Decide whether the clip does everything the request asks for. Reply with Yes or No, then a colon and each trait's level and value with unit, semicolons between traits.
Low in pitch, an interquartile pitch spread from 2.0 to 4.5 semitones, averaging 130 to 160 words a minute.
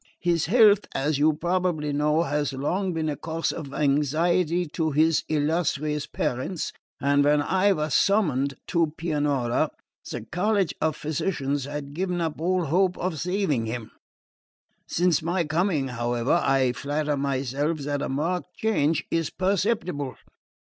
No: medium, 155 Hz; average, 3.7 semitones; average, 140 wpm